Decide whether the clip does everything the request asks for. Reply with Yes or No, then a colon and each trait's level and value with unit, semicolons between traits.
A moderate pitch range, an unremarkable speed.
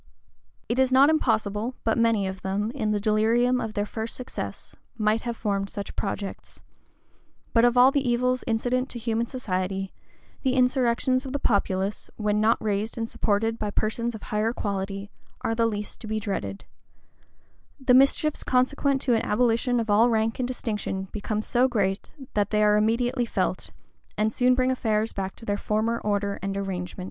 Yes: average, 3.2 semitones; average, 180 wpm